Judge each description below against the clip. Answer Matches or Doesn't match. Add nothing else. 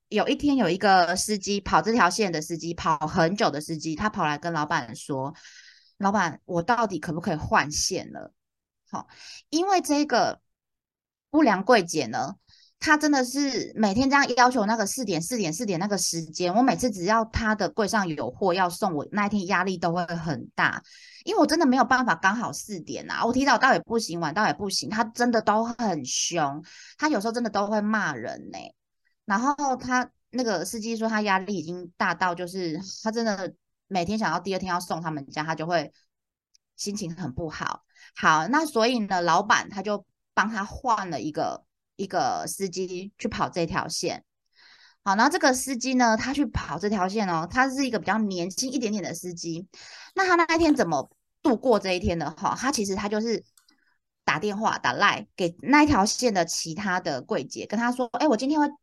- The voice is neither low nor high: Doesn't match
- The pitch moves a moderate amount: Doesn't match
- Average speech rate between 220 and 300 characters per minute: Matches